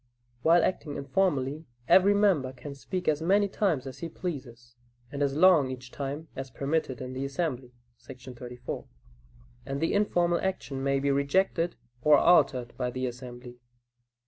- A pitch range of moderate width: Yes, average, 4.8 semitones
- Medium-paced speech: Yes, average, 155 wpm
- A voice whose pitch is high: No, medium, 140 Hz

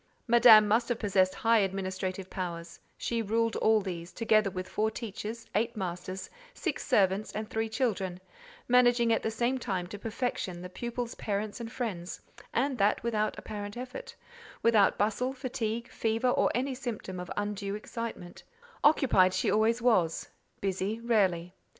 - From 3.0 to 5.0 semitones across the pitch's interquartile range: Yes, average, 3.6 semitones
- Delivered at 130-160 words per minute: Yes, average, 150 wpm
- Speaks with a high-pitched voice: Yes, high, 215 Hz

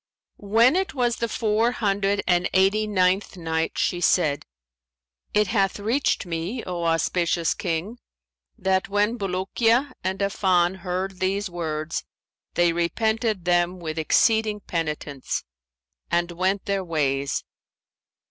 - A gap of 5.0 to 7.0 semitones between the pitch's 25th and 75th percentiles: No, average, 3.5 semitones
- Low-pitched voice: No, high, 190 Hz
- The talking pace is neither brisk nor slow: No, slow, 120 wpm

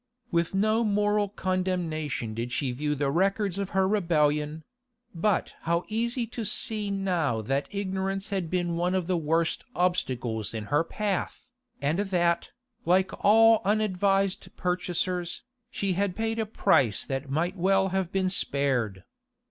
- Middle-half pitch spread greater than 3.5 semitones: Yes, average, 4.2 semitones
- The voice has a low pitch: No, medium, 185 Hz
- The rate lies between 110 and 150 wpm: Yes, average, 145 wpm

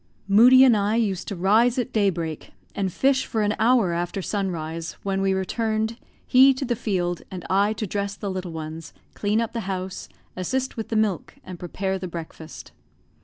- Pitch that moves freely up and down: No, average, 3.6 semitones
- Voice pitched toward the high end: Yes, high, 200 Hz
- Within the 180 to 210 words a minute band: Yes, average, 185 wpm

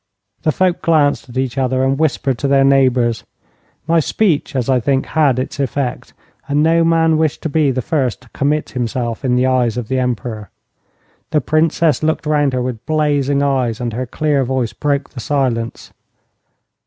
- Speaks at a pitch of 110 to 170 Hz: Yes, low, 135 Hz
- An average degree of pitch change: Yes, average, 3.1 semitones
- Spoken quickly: No, average, 180 wpm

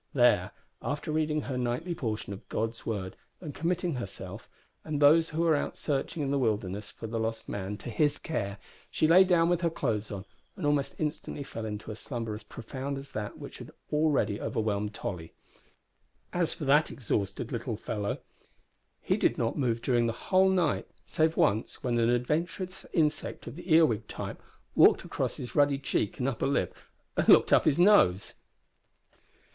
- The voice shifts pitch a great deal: Yes, wide, 6.3 semitones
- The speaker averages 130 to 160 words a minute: No, average, 180 wpm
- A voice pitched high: No, low, 135 Hz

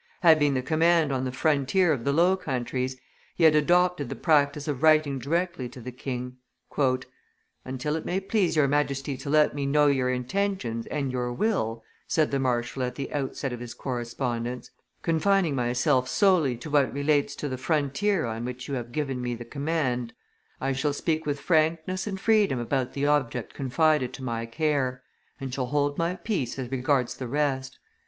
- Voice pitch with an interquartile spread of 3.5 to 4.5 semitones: Yes, average, 3.8 semitones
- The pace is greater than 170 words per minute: Yes, average, 180 wpm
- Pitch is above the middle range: No, medium, 140 Hz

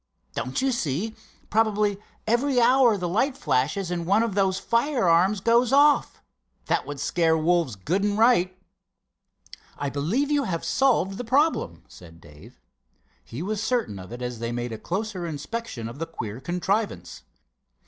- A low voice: No, high, 190 Hz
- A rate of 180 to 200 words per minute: No, average, 160 wpm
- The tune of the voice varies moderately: No, wide, 8.3 semitones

